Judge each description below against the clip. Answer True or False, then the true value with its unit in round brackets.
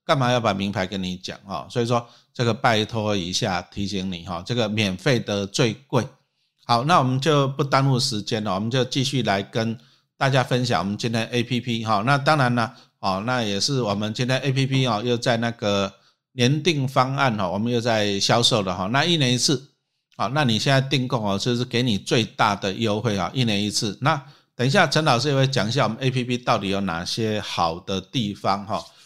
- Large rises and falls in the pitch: False (4.3 semitones)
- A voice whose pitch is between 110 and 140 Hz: True (120 Hz)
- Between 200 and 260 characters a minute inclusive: False (305 characters per minute)